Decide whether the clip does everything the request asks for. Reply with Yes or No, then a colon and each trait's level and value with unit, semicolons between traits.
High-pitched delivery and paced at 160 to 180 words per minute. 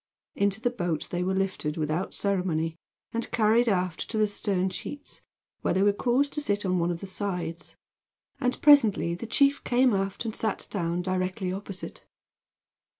Yes: high, 195 Hz; average, 170 wpm